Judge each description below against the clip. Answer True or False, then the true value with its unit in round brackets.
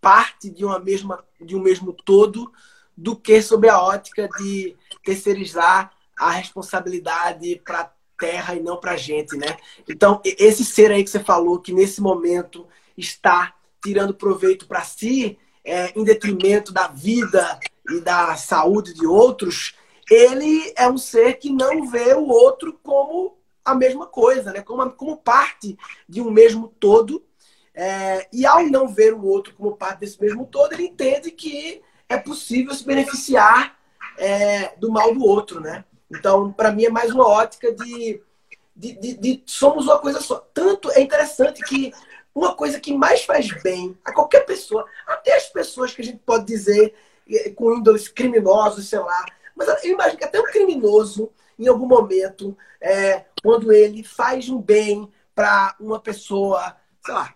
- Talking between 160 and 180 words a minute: True (165 wpm)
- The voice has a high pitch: True (220 Hz)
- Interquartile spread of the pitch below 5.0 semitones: False (5.3 semitones)